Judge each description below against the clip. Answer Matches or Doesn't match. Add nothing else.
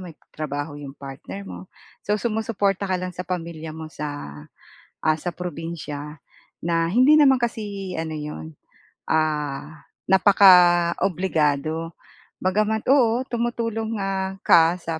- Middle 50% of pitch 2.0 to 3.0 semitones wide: Doesn't match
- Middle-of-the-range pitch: Matches